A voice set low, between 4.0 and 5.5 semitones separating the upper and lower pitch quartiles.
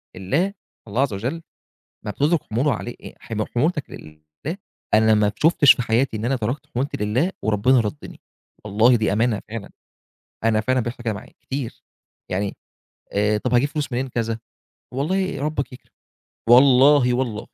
Yes: low, 120 Hz; average, 4.3 semitones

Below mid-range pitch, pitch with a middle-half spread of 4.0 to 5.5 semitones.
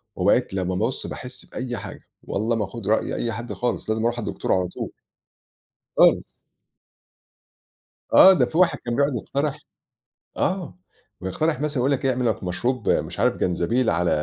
Yes: low, 120 Hz; average, 4.5 semitones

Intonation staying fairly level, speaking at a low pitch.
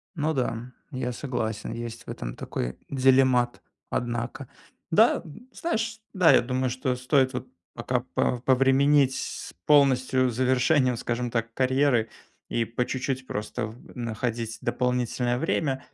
Yes: narrow, 2.0 semitones; low, 125 Hz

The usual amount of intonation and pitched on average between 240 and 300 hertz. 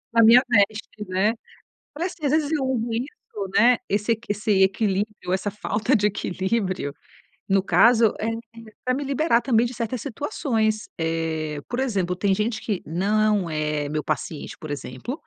No: average, 4.0 semitones; high, 215 Hz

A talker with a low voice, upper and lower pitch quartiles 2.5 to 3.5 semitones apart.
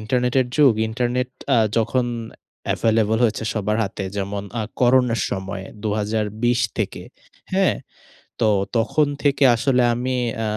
Yes: low, 115 Hz; average, 2.9 semitones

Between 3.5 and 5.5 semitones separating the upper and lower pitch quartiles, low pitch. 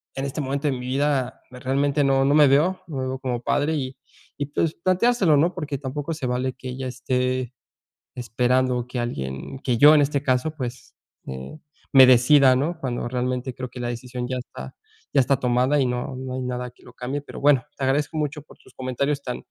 No: narrow, 2.4 semitones; low, 130 Hz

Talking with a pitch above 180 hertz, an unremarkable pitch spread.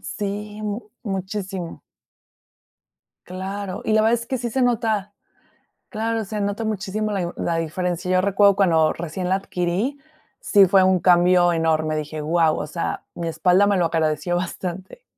Yes: high, 190 Hz; average, 3.3 semitones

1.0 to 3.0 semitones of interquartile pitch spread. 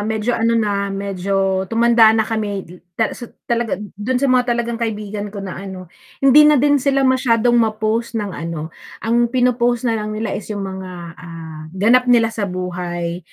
No: average, 3.5 semitones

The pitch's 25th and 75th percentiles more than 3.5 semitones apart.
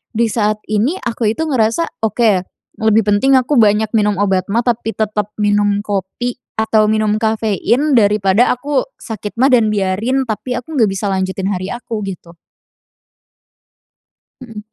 No: narrow, 2.6 semitones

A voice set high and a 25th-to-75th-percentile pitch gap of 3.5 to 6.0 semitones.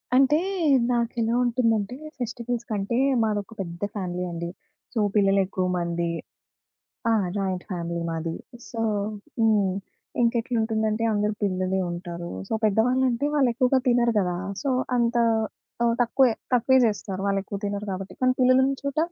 Yes: high, 220 Hz; average, 4.2 semitones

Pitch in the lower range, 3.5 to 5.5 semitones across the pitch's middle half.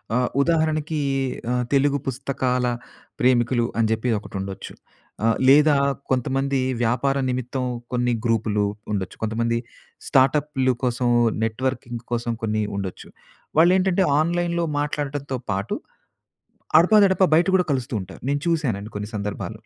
Yes: low, 130 Hz; average, 4.2 semitones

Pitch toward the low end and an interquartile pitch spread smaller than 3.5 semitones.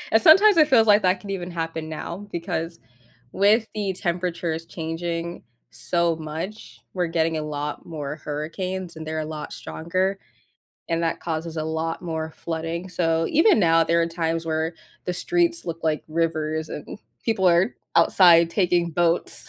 No: medium, 170 Hz; narrow, 2.4 semitones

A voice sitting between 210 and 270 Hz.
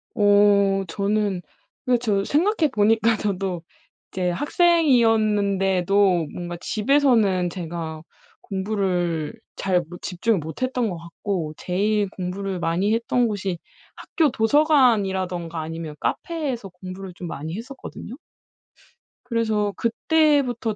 No: high, 200 Hz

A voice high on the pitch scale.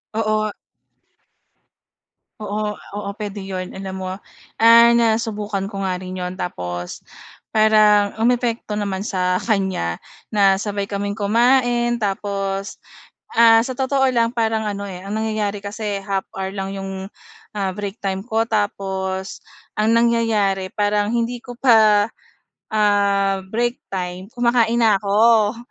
Yes: high, 205 Hz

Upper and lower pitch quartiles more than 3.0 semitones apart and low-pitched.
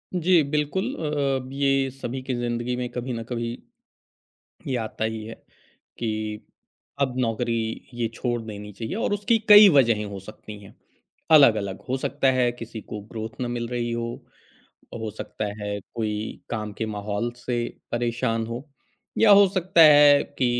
Yes: average, 3.5 semitones; low, 120 Hz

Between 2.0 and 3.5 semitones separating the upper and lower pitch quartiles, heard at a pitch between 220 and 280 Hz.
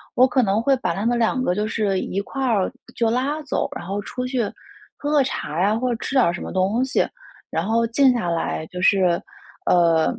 No: average, 5.3 semitones; high, 225 Hz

